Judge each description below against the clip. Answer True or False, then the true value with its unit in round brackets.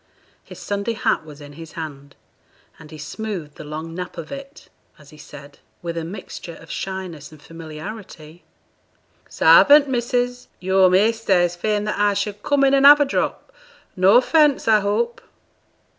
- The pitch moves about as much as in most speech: False (6.3 semitones)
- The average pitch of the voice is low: False (190 Hz)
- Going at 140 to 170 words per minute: True (165 wpm)